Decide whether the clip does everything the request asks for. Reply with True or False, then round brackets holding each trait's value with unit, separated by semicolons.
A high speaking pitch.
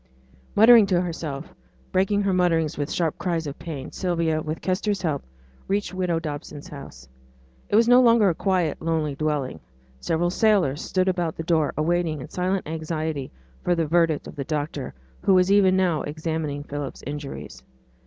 False (165 Hz)